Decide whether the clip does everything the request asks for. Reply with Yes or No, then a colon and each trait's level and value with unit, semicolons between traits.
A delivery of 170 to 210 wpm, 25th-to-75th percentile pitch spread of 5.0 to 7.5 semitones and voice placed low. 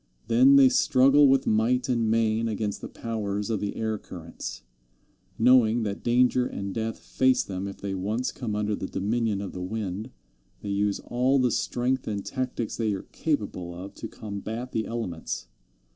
No: average, 175 wpm; average, 3.7 semitones; low, 110 Hz